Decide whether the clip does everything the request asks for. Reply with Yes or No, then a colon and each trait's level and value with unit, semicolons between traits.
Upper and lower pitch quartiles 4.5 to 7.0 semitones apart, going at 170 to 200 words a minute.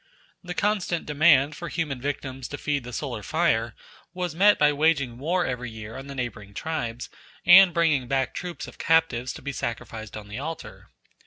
Yes: average, 5.1 semitones; average, 180 wpm